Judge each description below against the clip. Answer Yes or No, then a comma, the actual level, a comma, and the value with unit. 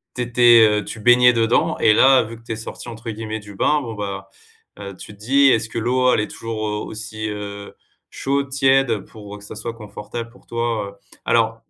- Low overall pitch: Yes, low, 115 Hz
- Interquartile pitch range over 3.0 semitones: No, narrow, 2.5 semitones